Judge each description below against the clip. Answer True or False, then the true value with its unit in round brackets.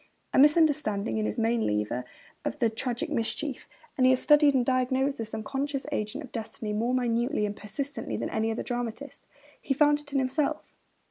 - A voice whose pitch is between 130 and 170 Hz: False (255 Hz)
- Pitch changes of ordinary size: True (4.2 semitones)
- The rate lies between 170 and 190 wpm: True (185 wpm)